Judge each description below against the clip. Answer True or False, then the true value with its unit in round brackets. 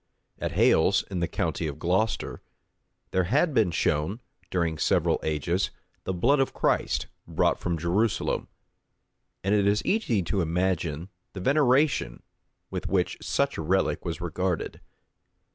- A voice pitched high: False (95 Hz)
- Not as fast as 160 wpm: True (140 wpm)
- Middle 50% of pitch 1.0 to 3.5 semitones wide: False (4.3 semitones)